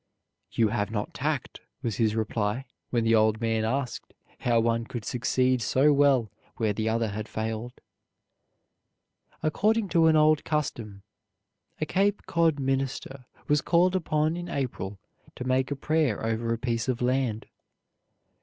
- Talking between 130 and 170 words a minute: Yes, average, 150 wpm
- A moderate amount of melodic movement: Yes, average, 4.8 semitones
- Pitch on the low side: Yes, low, 125 Hz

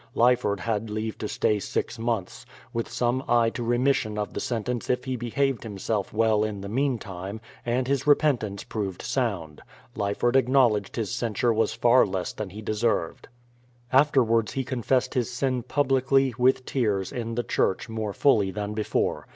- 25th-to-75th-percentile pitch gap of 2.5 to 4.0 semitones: Yes, average, 3.1 semitones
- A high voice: No, low, 115 Hz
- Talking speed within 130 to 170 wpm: No, average, 180 wpm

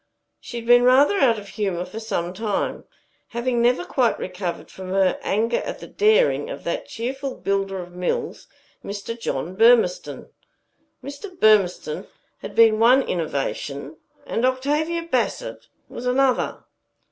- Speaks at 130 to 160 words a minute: Yes, average, 140 wpm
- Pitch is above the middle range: Yes, high, 230 Hz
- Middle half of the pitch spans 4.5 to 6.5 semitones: Yes, wide, 5.5 semitones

